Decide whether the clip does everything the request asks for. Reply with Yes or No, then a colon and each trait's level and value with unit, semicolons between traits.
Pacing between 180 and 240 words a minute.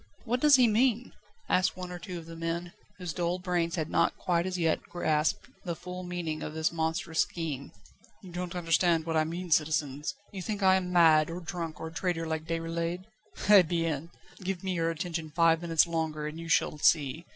Yes: fast, 205 wpm